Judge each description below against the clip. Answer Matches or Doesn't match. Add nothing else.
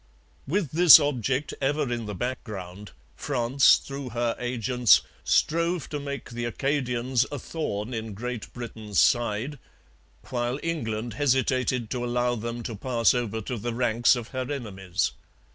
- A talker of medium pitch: Doesn't match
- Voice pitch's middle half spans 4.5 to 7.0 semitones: Doesn't match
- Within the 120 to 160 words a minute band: Matches